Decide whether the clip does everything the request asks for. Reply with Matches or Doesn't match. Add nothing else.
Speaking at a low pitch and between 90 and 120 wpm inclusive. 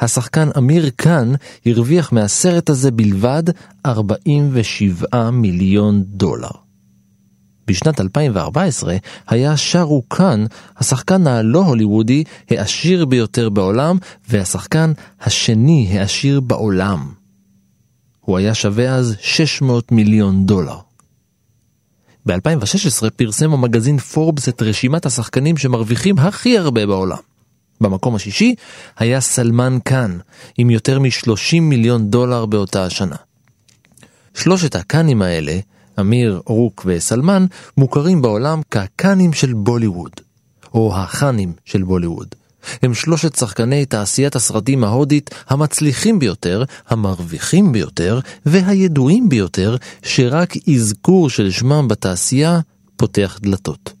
Matches